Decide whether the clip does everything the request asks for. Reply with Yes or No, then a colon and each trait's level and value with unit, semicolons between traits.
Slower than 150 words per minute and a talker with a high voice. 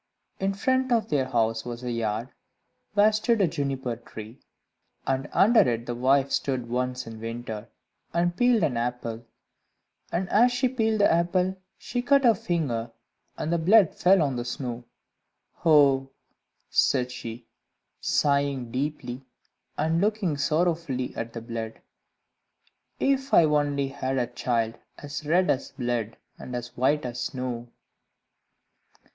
No: average, 140 wpm; low, 135 Hz